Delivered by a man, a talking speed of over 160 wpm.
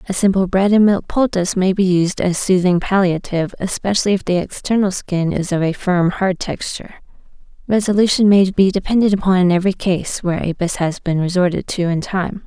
No: female; average, 190 wpm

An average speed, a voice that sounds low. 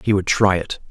No: fast, 265 wpm; very low, 95 Hz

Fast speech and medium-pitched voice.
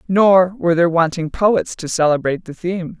No: average, 180 wpm; medium, 175 Hz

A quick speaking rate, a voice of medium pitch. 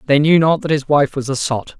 Yes: fast, 300 wpm; medium, 145 Hz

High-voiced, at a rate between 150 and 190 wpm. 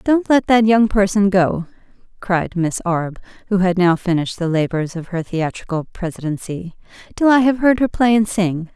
Yes: high, 195 Hz; average, 185 wpm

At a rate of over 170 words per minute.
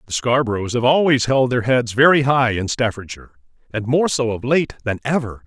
Yes: average, 200 wpm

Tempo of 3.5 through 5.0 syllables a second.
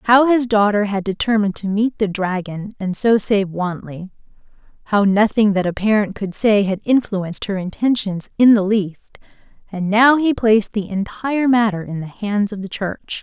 Yes: 4.8 syllables/s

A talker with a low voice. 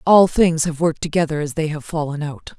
No: medium, 160 Hz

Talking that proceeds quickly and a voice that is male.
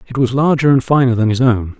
Yes: fast, 265 wpm; male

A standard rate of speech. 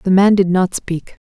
No: fast, 240 wpm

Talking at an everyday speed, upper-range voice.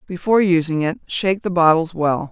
No: average, 180 wpm; medium, 170 Hz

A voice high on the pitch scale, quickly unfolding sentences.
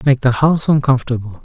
No: low, 130 Hz; fast, 210 wpm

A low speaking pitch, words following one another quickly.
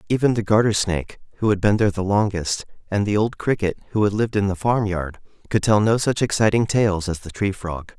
Yes: low, 100 Hz; fast, 235 wpm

